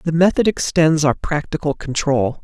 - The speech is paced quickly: No, average, 150 wpm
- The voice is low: No, medium, 150 Hz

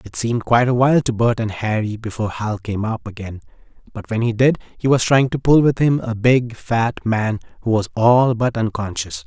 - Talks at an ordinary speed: No, fast, 220 wpm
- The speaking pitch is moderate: No, low, 115 Hz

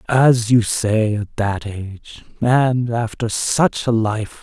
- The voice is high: No, low, 115 Hz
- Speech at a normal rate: Yes, average, 150 wpm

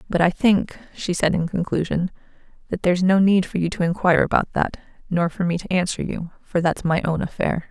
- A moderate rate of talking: No, fast, 220 wpm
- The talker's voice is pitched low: No, medium, 180 Hz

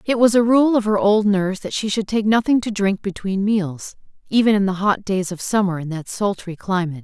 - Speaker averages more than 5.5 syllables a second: No, 5.4 syllables/s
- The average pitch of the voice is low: No, high, 200 Hz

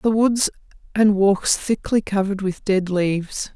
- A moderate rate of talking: Yes, average, 150 wpm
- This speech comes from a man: No, female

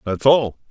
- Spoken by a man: Yes, male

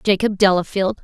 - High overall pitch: Yes, high, 195 Hz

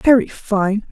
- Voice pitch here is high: Yes, high, 215 Hz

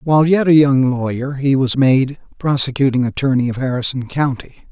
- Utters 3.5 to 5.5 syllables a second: Yes, 5.3 syllables/s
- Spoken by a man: Yes, male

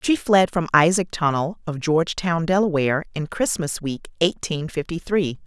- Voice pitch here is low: No, medium, 165 Hz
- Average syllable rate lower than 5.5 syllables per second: Yes, 4.9 syllables/s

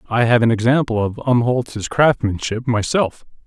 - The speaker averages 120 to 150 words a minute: Yes, average, 140 wpm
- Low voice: Yes, low, 120 Hz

